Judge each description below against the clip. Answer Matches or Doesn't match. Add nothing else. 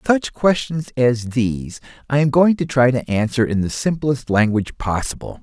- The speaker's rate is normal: Matches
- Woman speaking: Doesn't match